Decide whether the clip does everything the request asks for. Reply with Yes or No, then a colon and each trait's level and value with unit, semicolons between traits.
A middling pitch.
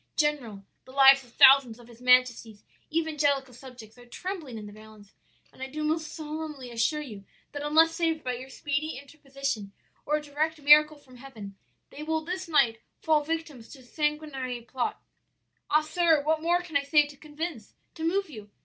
No: very high, 285 Hz